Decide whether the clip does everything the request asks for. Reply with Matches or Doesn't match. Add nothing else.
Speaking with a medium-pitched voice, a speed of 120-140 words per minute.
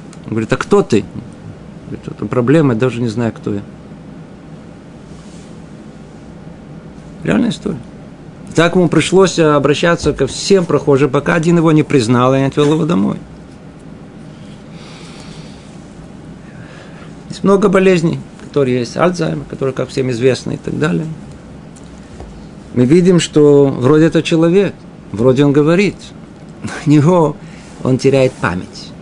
Matches